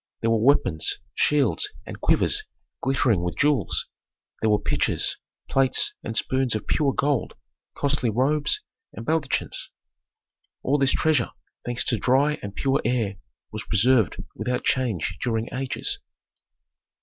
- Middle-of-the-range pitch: No, low, 125 Hz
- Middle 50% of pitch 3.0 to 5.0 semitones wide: Yes, average, 4.0 semitones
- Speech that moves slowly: Yes, slow, 130 wpm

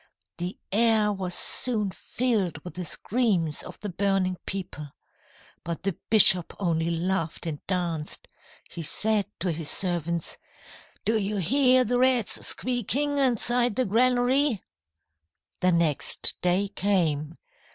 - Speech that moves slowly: Yes, slow, 125 wpm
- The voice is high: Yes, high, 195 Hz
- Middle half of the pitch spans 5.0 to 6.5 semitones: Yes, wide, 5.5 semitones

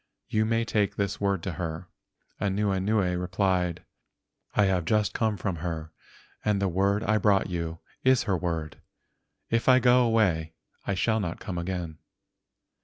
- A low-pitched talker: Yes, very low, 95 Hz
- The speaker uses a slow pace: No, average, 155 wpm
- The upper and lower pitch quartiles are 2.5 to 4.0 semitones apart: Yes, average, 3.4 semitones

